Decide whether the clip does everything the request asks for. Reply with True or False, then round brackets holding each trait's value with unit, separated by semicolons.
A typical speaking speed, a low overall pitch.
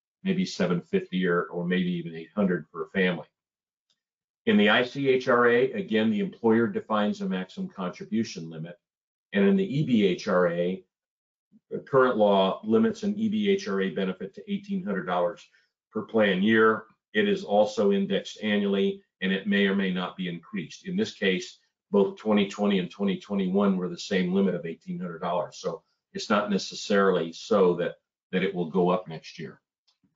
True (150 wpm; 105 Hz)